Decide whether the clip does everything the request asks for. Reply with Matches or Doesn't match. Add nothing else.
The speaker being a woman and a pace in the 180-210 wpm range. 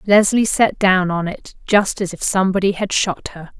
Matches